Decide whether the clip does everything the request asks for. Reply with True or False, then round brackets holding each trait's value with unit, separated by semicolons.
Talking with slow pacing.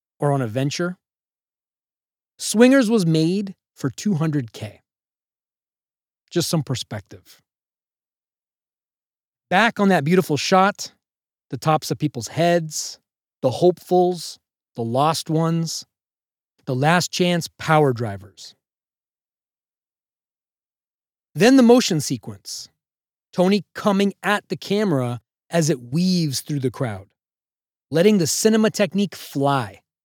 True (105 wpm)